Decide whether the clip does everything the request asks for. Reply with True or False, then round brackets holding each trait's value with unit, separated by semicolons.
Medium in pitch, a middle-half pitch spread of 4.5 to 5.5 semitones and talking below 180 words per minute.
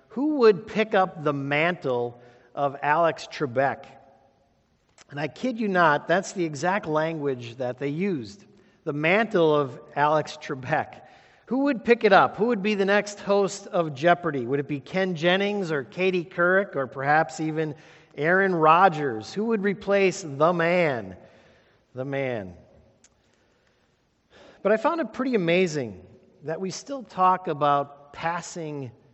True (170 Hz; 5.2 semitones; 145 wpm)